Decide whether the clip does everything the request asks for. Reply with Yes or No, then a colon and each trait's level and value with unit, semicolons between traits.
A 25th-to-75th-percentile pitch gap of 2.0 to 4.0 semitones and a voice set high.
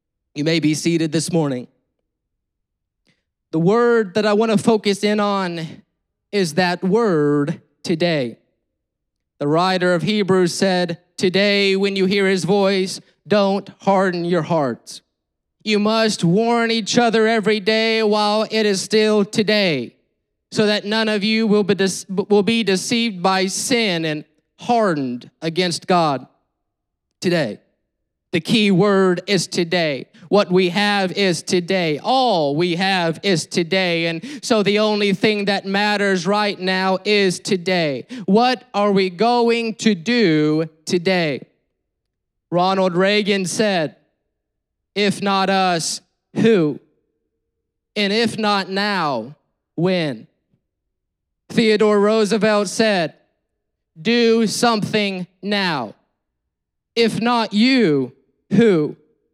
Yes: average, 3.7 semitones; high, 195 Hz